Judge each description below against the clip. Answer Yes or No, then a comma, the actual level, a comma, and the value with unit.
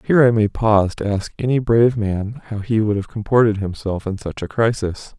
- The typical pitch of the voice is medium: No, low, 110 Hz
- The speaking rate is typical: No, fast, 220 wpm